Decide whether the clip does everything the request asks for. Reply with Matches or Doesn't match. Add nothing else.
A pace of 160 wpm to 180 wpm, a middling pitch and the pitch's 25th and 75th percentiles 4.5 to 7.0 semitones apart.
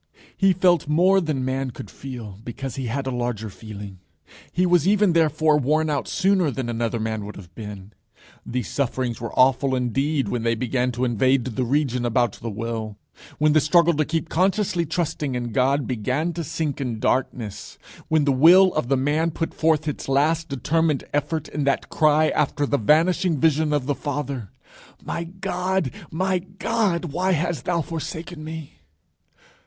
Matches